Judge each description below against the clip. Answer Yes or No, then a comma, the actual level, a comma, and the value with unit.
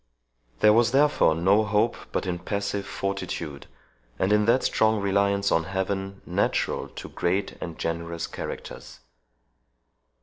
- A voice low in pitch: Yes, low, 100 Hz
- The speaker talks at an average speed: No, slow, 130 wpm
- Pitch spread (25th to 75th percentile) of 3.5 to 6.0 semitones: No, average, 3.0 semitones